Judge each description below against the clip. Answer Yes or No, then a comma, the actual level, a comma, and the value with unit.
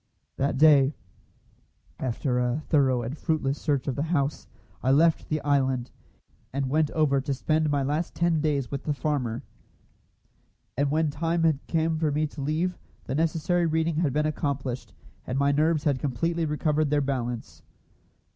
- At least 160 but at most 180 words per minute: Yes, average, 165 wpm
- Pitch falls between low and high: Yes, medium, 145 Hz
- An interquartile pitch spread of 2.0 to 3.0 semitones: Yes, narrow, 2.5 semitones